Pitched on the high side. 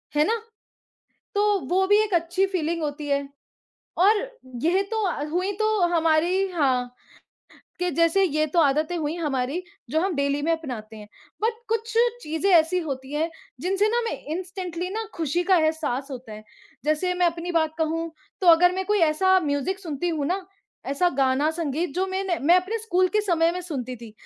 Yes: very high, 335 Hz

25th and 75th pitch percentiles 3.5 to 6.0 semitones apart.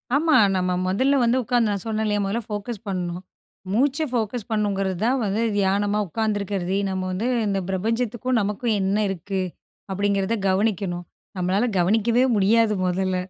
No: average, 3.1 semitones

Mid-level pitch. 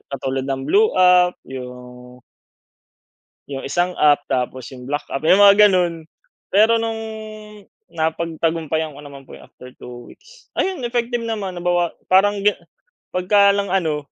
Yes: medium, 170 Hz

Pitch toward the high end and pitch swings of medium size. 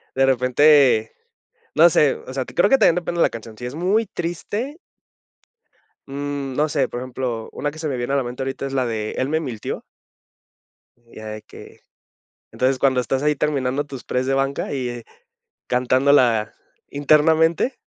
No: low, 135 Hz; average, 3.3 semitones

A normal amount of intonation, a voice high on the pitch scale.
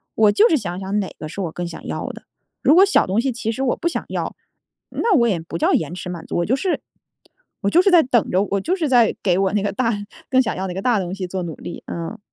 No: wide, 6.2 semitones; high, 205 Hz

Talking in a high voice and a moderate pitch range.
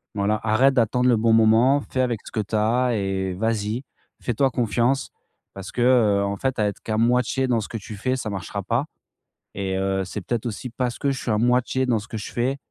No: low, 115 Hz; average, 3.2 semitones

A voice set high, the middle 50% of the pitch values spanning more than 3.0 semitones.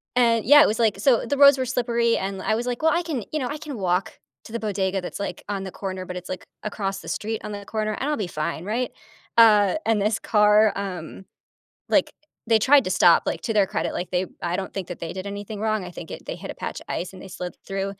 Yes: high, 210 Hz; average, 3.6 semitones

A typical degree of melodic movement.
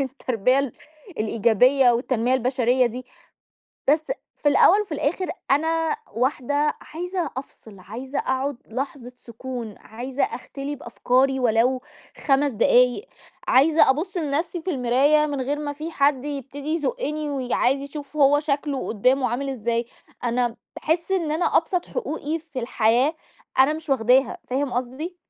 Yes: average, 3.4 semitones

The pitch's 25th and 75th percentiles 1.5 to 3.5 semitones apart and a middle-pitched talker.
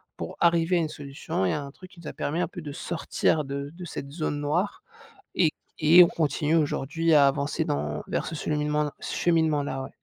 Yes: average, 2.9 semitones; medium, 150 Hz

